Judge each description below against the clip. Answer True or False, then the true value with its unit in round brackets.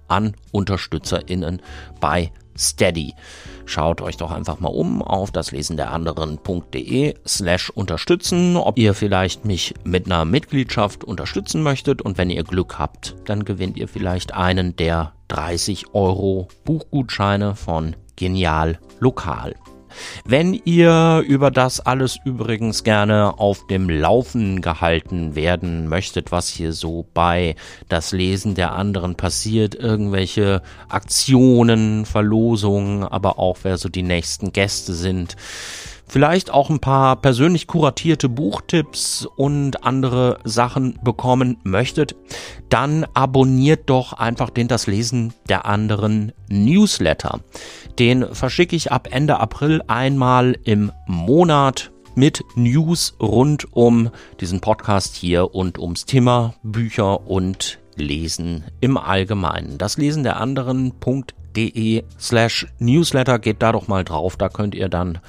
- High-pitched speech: False (105 Hz)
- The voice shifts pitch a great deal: True (5.9 semitones)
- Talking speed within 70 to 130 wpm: True (125 wpm)